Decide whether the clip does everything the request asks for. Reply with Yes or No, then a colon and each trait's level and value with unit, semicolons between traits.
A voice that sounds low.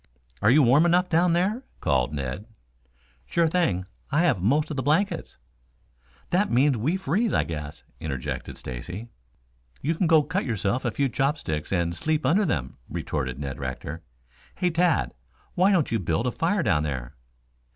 Yes: low, 130 Hz